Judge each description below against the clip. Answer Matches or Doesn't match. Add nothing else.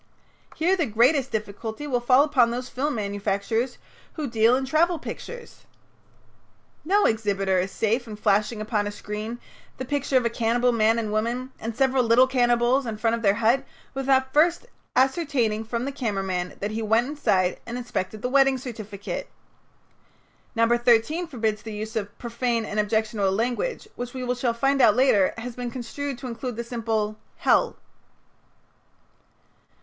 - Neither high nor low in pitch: Doesn't match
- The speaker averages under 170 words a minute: Matches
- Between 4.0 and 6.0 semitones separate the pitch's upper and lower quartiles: Doesn't match